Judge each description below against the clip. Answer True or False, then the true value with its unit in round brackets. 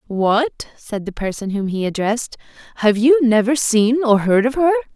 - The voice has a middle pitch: False (235 Hz)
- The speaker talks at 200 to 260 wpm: False (180 wpm)